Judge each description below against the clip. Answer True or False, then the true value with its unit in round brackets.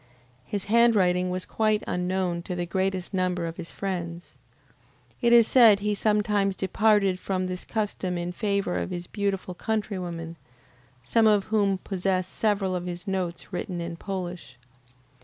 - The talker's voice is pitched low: False (190 Hz)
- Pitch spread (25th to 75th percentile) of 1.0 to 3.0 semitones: True (2.6 semitones)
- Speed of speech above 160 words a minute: False (150 wpm)